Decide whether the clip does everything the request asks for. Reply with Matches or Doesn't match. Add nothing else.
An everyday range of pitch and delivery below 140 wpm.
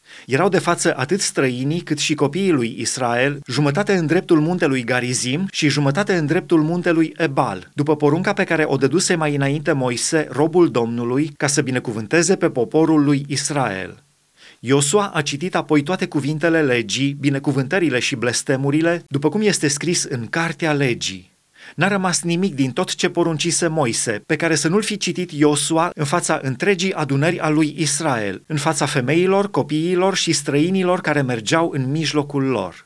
Doesn't match